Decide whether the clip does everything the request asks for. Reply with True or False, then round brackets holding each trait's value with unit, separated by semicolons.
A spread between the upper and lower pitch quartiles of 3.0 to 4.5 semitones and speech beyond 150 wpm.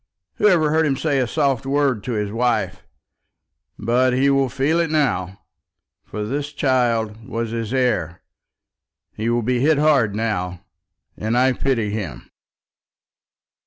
False (4.2 semitones; 145 wpm)